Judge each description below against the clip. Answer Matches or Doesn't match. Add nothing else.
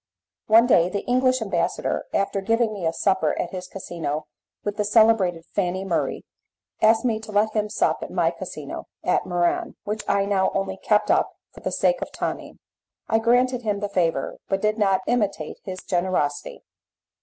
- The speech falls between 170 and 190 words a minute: Matches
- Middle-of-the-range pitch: Doesn't match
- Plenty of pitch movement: Doesn't match